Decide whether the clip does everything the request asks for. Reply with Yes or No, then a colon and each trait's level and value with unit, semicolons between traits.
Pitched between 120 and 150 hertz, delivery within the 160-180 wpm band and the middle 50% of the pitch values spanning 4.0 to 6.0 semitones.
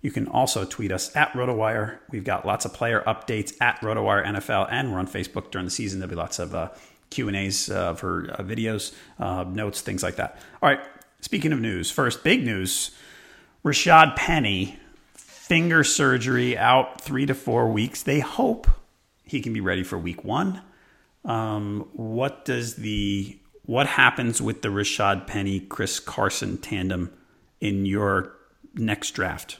No: low, 105 Hz; average, 170 wpm; average, 4.7 semitones